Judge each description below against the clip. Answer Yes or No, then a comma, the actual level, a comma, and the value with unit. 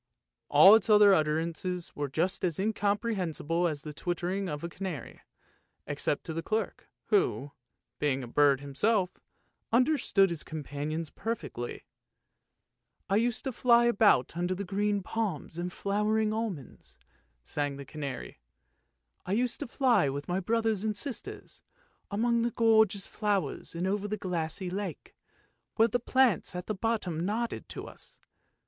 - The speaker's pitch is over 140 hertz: Yes, high, 190 Hz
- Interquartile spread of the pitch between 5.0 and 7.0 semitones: Yes, wide, 5.5 semitones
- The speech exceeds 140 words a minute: Yes, average, 150 wpm